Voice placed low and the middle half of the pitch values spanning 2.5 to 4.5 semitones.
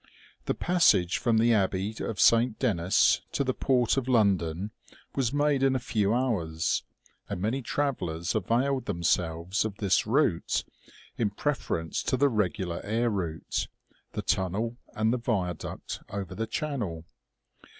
No: low, 110 Hz; wide, 5.5 semitones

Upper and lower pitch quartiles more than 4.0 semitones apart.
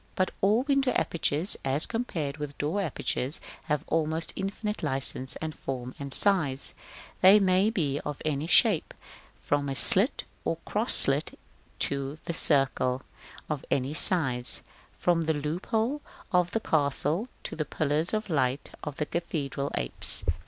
Yes: average, 4.9 semitones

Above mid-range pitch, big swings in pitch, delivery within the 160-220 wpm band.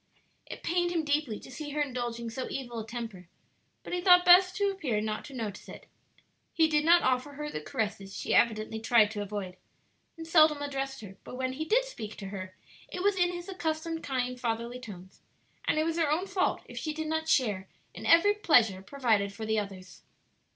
Yes: very high, 260 Hz; wide, 6.9 semitones; fast, 205 wpm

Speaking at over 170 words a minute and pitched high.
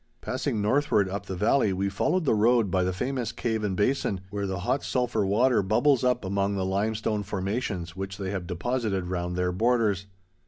No: average, 190 wpm; low, 100 Hz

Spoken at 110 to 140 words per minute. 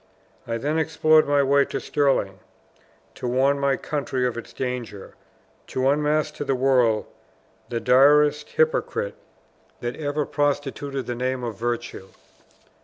Yes: slow, 135 wpm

